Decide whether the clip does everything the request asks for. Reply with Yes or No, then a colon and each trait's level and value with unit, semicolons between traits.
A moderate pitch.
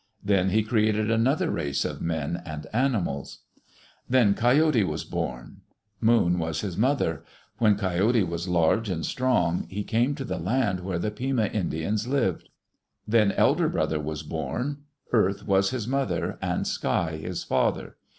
No: low, 100 Hz